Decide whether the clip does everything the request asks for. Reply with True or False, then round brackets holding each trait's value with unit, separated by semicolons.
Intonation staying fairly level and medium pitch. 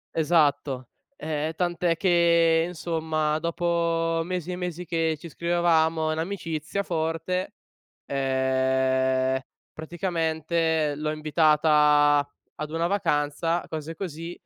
True (2.0 semitones; 160 Hz)